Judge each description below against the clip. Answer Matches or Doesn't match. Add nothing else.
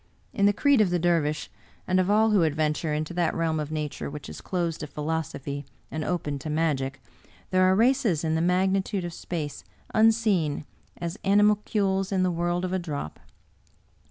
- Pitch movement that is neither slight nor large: Matches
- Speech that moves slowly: Doesn't match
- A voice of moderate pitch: Matches